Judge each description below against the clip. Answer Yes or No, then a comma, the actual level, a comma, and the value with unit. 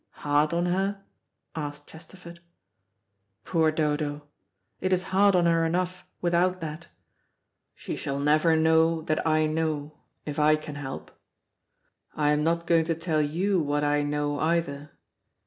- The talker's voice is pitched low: No, medium, 160 Hz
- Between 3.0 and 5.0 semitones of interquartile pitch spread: No, narrow, 2.5 semitones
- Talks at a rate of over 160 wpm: No, average, 145 wpm